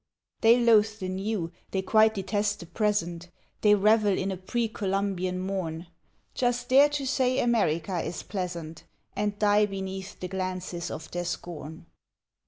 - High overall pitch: Yes, high, 195 Hz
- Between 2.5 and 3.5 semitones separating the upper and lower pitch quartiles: Yes, average, 3.2 semitones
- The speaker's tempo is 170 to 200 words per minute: No, average, 150 wpm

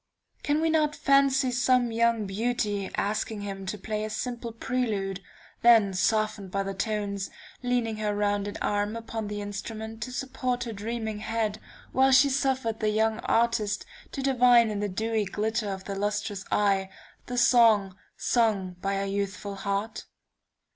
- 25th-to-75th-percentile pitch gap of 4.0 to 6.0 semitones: No, average, 2.8 semitones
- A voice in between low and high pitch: No, high, 215 Hz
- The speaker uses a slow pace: No, average, 155 wpm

